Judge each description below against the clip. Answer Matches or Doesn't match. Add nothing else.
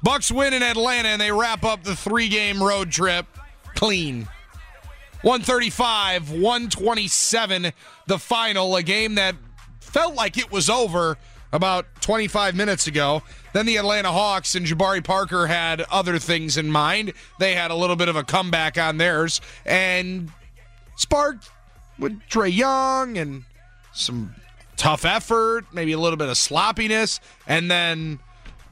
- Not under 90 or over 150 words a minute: Matches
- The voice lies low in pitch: Doesn't match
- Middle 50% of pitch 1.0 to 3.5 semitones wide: Doesn't match